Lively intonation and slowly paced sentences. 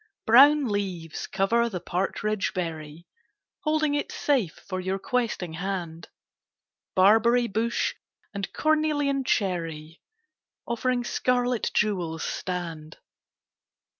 Yes: wide, 5.9 semitones; slow, 100 wpm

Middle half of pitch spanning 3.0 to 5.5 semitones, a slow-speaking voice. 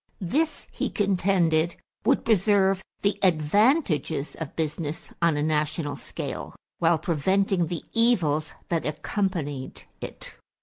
Yes: average, 4.3 semitones; slow, 115 wpm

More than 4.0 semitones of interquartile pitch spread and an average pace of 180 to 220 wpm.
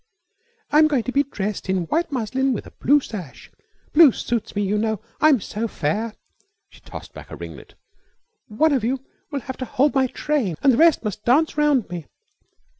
Yes: average, 5.3 semitones; average, 190 wpm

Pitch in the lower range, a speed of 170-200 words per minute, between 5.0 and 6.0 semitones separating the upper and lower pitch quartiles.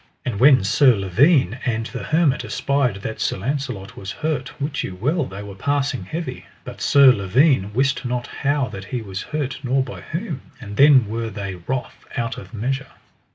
Yes: low, 125 Hz; average, 185 wpm; wide, 5.5 semitones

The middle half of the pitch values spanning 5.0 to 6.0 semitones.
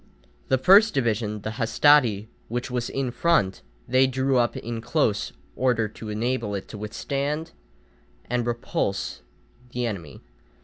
No: average, 3.5 semitones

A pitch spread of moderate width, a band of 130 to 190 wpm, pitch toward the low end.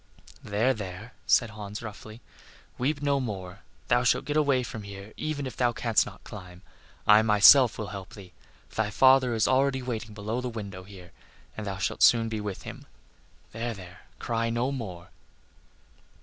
Yes: average, 3.8 semitones; average, 170 wpm; low, 110 Hz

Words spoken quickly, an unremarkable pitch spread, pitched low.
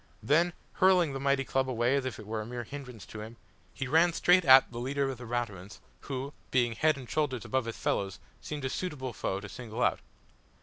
Yes: fast, 220 wpm; average, 3.4 semitones; low, 130 Hz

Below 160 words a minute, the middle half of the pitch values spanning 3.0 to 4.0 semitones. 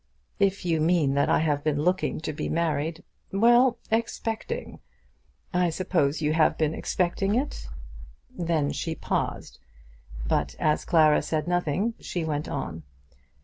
Yes: average, 145 wpm; average, 3.6 semitones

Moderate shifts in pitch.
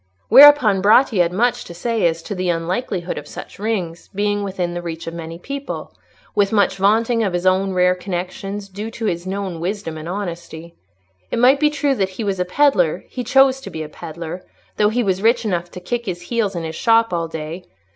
Yes: average, 4.5 semitones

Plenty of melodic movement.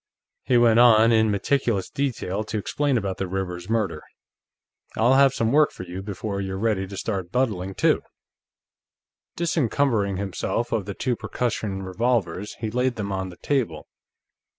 No: average, 4.0 semitones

